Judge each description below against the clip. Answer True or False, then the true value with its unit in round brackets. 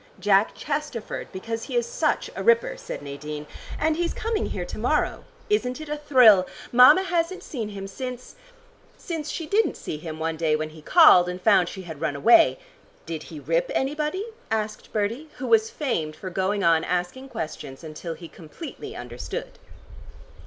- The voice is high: True (215 Hz)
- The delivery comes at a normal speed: True (175 wpm)